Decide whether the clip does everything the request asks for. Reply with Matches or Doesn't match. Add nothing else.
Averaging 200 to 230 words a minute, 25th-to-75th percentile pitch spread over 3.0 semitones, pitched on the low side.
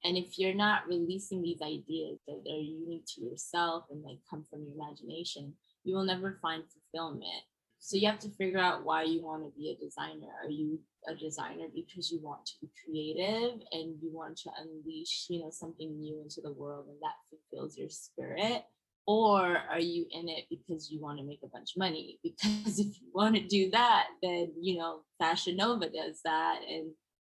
Doesn't match